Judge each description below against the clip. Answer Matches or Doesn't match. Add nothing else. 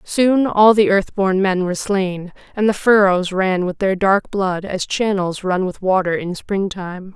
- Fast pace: Doesn't match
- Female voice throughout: Matches